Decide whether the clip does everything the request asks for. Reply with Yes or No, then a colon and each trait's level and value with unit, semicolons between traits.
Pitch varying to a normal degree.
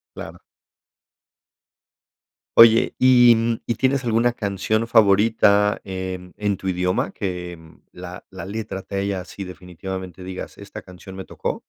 Yes: average, 3.3 semitones